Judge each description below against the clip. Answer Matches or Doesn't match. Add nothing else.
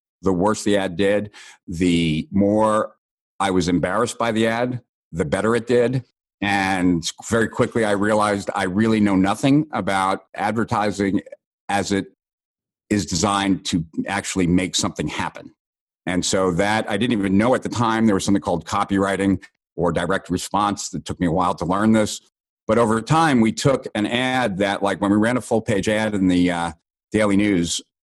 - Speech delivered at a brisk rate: Doesn't match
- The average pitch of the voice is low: Matches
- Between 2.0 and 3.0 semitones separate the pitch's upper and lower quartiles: Matches